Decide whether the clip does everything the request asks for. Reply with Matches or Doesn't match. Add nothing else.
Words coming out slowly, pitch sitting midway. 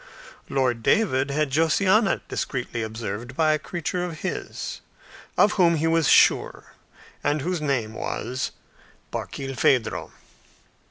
Matches